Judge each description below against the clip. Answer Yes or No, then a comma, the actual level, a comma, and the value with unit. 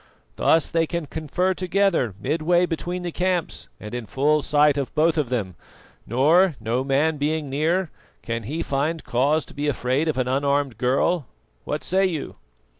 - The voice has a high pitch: No, medium, 150 Hz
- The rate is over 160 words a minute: Yes, average, 170 wpm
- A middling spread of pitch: Yes, average, 4.0 semitones